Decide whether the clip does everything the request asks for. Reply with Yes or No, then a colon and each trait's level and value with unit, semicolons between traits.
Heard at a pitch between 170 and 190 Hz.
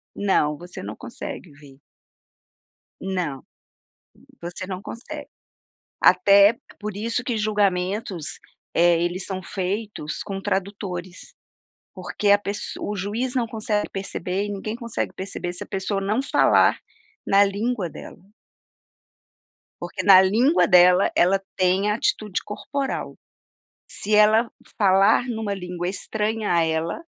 No: high, 200 Hz